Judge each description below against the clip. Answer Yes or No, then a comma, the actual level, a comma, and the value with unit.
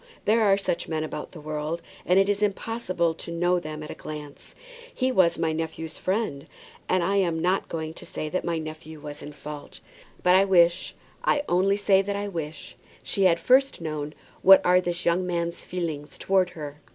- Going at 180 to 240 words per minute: Yes, average, 200 wpm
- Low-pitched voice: No, medium, 170 Hz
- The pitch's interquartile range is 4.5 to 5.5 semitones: No, average, 3.4 semitones